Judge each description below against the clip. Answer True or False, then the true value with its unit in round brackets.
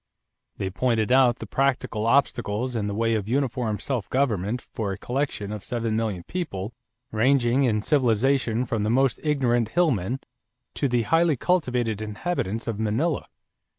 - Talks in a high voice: False (120 Hz)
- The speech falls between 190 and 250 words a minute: False (155 wpm)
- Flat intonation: False (3.8 semitones)